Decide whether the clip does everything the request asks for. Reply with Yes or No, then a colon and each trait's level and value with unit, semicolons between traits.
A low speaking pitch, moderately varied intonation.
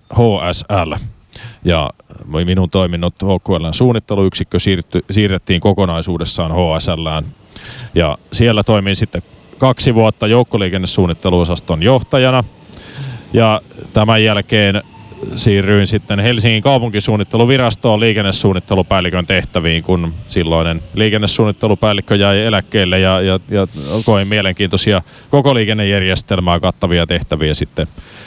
Yes: low, 100 Hz; average, 3.6 semitones